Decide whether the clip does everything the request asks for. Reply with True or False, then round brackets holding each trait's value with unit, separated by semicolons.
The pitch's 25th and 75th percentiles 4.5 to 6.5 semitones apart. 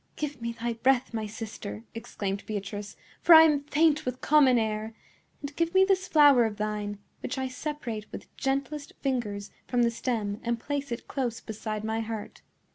True (4.8 semitones)